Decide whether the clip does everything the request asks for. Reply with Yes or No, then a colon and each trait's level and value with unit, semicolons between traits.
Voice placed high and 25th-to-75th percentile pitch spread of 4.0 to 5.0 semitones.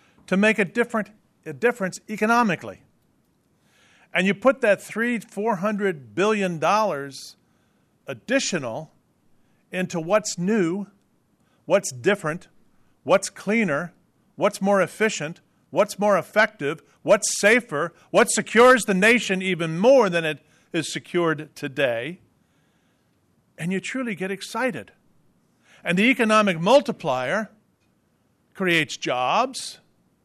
Yes: high, 200 Hz; average, 4.3 semitones